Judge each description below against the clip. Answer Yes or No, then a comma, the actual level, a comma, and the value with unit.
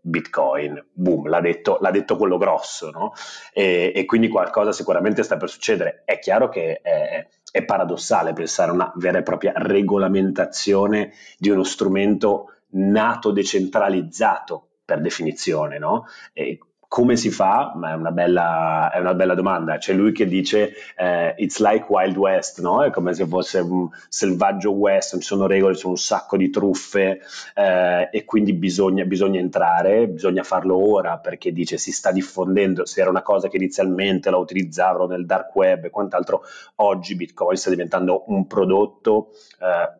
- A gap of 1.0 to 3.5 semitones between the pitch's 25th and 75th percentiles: Yes, narrow, 2.4 semitones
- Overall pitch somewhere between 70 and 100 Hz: Yes, very low, 95 Hz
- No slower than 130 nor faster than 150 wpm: No, average, 165 wpm